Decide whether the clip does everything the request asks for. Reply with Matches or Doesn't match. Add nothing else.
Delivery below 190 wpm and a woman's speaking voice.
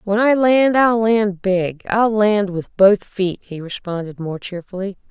Matches